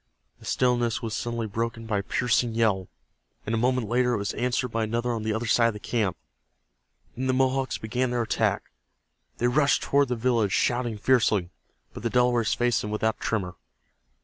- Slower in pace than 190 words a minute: No, average, 195 wpm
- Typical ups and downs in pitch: No, narrow, 2.0 semitones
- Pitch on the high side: No, low, 115 Hz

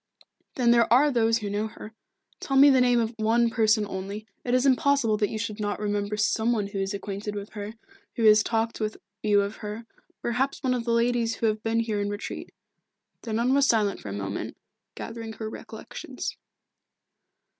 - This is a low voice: No, high, 220 Hz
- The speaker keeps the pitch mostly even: Yes, narrow, 2.2 semitones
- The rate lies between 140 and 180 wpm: No, average, 200 wpm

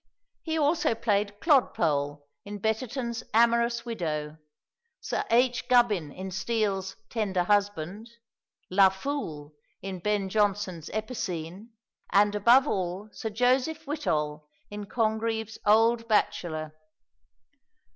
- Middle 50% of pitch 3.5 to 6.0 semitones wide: Yes, average, 4.3 semitones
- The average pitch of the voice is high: Yes, high, 210 Hz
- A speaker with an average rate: No, slow, 105 wpm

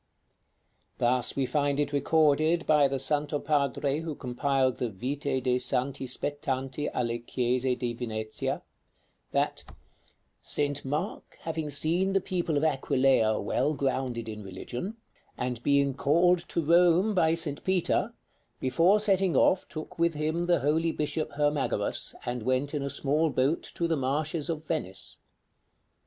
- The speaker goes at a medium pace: Yes, average, 145 wpm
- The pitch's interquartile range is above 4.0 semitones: No, average, 3.7 semitones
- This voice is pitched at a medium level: Yes, medium, 145 Hz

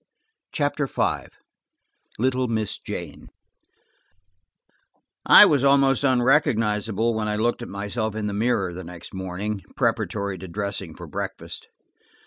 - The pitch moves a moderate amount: Yes, average, 4.0 semitones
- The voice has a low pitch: Yes, low, 110 Hz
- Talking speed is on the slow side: Yes, slow, 120 wpm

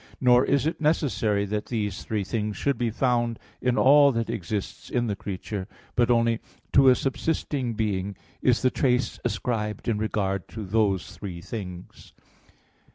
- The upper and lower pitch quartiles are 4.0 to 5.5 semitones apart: No, average, 3.5 semitones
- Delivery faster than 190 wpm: No, average, 160 wpm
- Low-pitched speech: Yes, low, 115 Hz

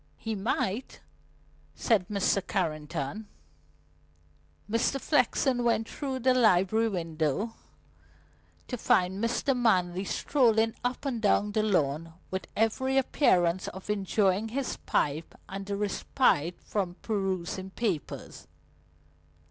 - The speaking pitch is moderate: No, high, 205 Hz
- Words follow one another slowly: Yes, slow, 110 wpm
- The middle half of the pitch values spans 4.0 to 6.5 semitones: Yes, average, 4.3 semitones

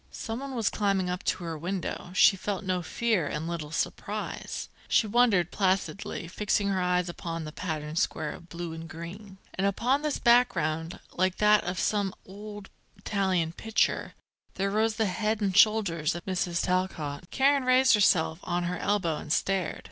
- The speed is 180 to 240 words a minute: No, average, 170 wpm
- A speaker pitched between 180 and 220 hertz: Yes, high, 190 Hz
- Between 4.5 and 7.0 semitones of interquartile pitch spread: No, average, 3.6 semitones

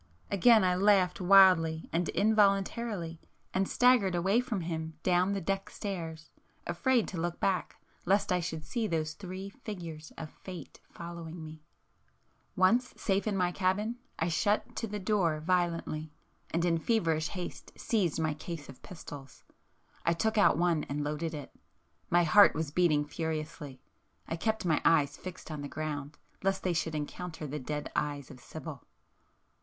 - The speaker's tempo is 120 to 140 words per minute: No, average, 160 wpm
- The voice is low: No, medium, 175 Hz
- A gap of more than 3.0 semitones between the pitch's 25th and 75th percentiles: Yes, average, 3.7 semitones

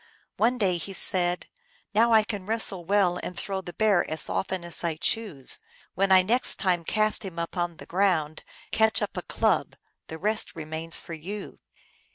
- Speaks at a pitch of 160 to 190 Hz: Yes, medium, 185 Hz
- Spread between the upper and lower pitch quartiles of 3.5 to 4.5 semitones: Yes, average, 3.8 semitones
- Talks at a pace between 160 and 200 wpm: Yes, average, 185 wpm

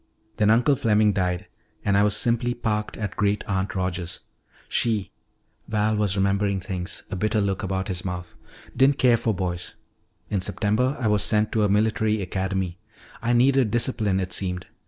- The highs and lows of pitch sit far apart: No, average, 2.8 semitones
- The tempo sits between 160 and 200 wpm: Yes, average, 170 wpm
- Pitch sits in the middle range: No, low, 105 Hz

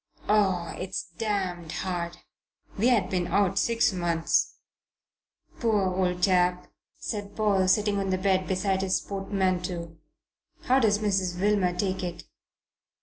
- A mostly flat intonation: Yes, narrow, 2.3 semitones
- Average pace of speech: No, slow, 130 wpm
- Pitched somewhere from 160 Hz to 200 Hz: Yes, high, 190 Hz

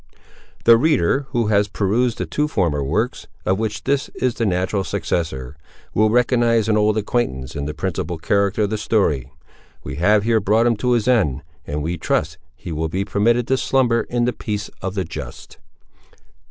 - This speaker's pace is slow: No, average, 185 wpm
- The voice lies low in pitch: Yes, low, 105 Hz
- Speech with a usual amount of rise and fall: No, wide, 5.7 semitones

